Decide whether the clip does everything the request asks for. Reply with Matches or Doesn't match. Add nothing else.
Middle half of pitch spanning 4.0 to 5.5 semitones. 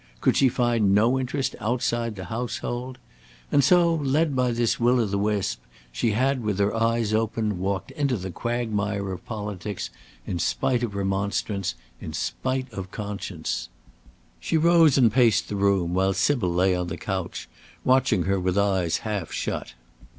Matches